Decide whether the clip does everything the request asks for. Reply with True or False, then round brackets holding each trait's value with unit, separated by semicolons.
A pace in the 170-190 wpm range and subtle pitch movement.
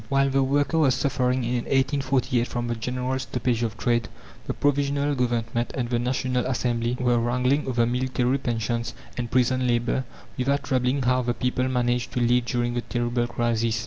True (175 wpm; 1.6 semitones)